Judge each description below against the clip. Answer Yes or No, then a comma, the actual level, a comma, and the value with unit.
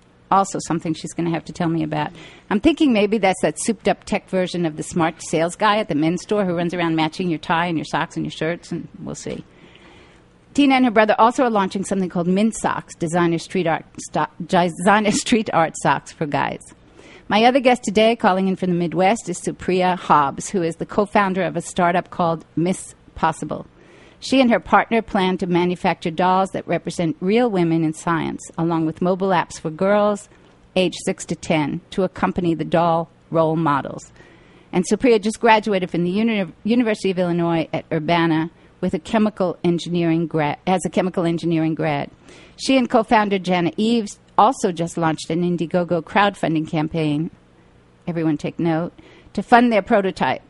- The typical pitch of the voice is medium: Yes, medium, 180 Hz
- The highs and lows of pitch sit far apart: No, average, 3.7 semitones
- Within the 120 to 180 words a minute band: No, average, 190 wpm